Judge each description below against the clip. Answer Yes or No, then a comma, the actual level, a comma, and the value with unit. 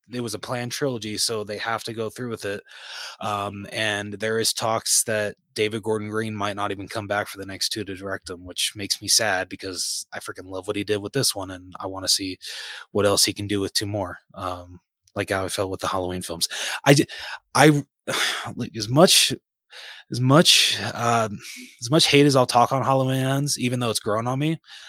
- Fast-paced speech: Yes, fast, 220 wpm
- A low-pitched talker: Yes, low, 105 Hz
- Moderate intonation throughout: Yes, average, 3.6 semitones